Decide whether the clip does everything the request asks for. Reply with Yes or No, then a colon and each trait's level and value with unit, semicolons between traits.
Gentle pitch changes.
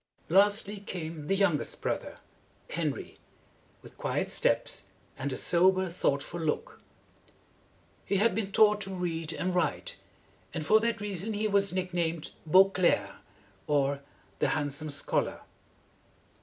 No: average, 4.2 semitones